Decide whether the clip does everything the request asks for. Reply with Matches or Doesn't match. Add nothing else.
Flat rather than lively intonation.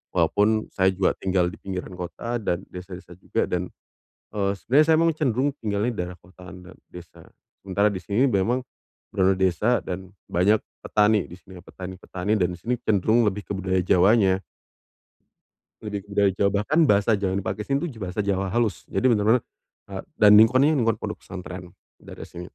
Doesn't match